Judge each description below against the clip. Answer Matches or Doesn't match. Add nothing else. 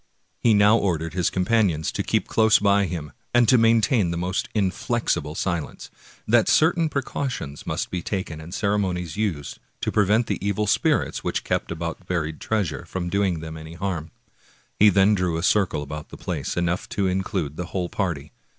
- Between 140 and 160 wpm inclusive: Doesn't match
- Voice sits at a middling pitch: Doesn't match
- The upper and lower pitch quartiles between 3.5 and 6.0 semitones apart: Matches